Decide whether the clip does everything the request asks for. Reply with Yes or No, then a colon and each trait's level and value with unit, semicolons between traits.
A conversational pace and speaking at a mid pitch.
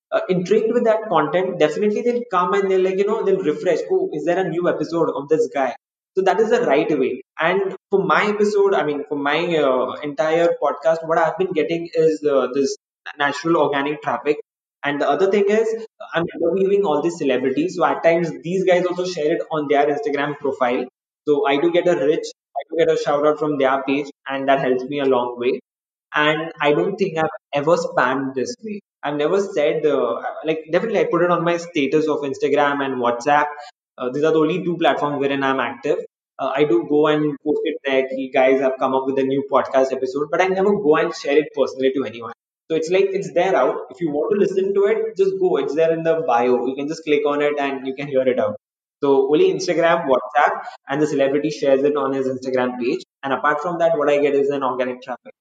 No: fast, 235 wpm; medium, 155 Hz